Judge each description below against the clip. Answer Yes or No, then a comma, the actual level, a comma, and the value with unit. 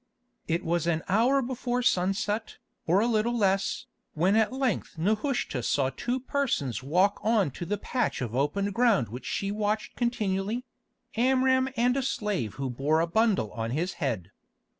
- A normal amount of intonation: No, wide, 6.8 semitones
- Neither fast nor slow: Yes, average, 160 wpm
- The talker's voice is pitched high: Yes, high, 200 Hz